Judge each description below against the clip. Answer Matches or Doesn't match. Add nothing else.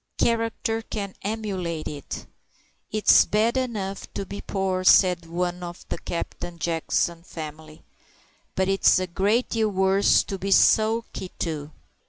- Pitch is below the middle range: Doesn't match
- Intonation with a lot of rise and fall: Doesn't match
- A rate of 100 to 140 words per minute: Matches